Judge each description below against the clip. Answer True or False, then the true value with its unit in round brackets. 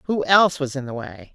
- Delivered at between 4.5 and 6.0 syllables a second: True (5.9 syllables/s)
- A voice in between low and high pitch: True (150 Hz)